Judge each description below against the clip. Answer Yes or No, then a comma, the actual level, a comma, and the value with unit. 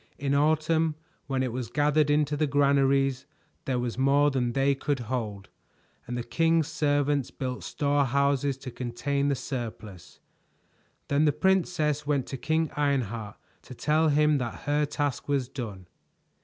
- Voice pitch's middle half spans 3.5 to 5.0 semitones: No, average, 2.7 semitones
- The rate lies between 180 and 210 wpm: No, average, 150 wpm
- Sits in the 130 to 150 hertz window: Yes, medium, 140 Hz